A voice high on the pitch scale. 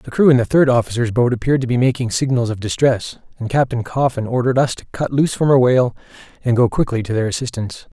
No: low, 125 Hz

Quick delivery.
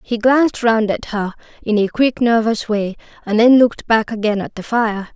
Yes: fast, 210 wpm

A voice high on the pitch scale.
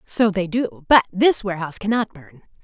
Yes: high, 200 Hz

